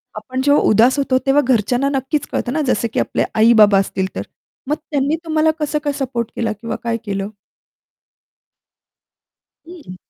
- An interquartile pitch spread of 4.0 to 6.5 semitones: Yes, average, 4.5 semitones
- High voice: Yes, very high, 255 Hz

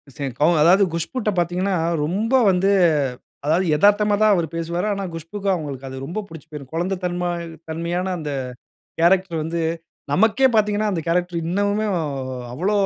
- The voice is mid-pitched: Yes, medium, 180 Hz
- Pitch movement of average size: Yes, average, 3.6 semitones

